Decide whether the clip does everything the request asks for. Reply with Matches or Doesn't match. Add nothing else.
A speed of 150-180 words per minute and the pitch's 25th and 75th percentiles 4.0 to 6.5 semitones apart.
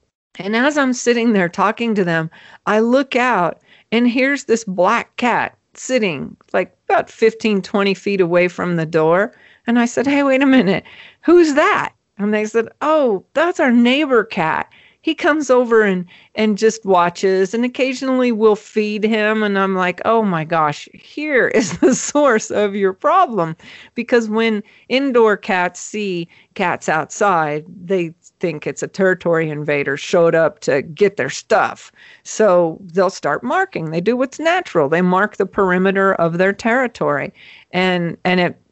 Matches